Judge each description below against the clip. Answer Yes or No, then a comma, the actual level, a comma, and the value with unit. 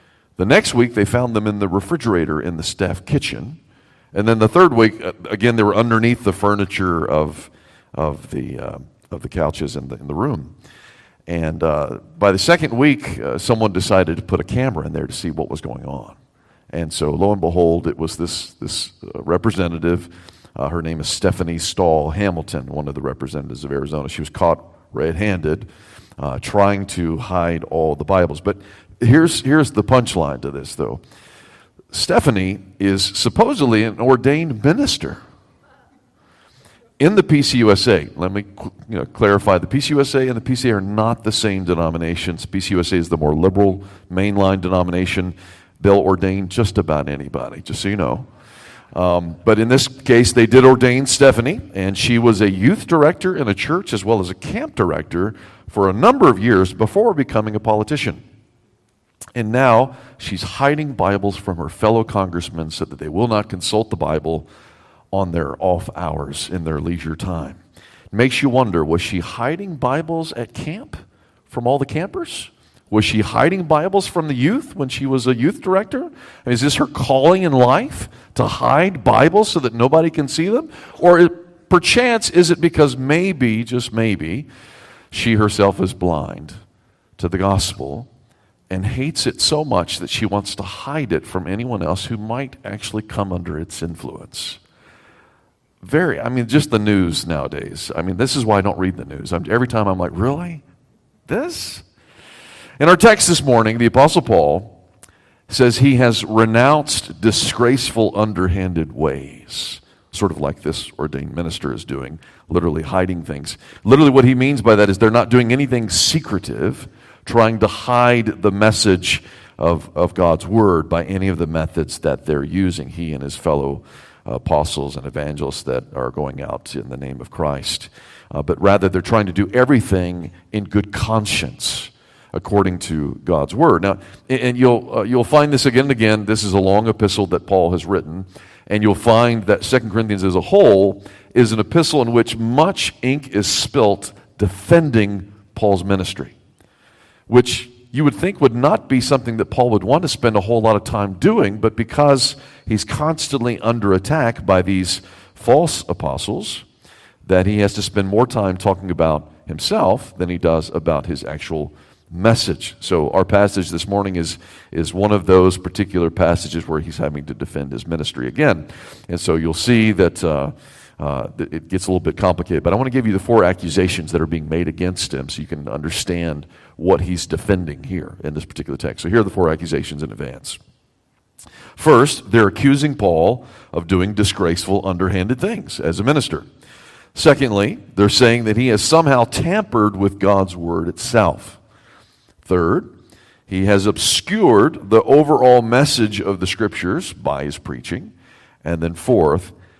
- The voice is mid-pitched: No, low, 100 Hz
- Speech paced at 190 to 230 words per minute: No, average, 175 wpm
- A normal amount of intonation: No, wide, 5.8 semitones